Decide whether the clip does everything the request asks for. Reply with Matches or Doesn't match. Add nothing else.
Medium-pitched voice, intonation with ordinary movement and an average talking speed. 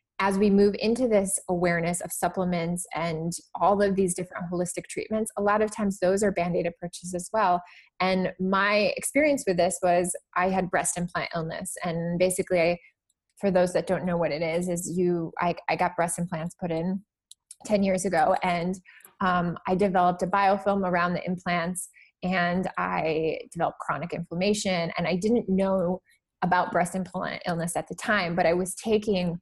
Doesn't match